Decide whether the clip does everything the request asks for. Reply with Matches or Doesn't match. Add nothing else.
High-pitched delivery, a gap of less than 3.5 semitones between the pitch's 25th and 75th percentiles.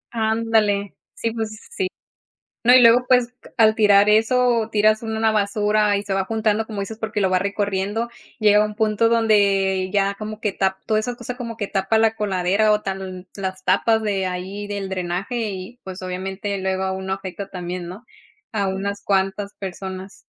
Matches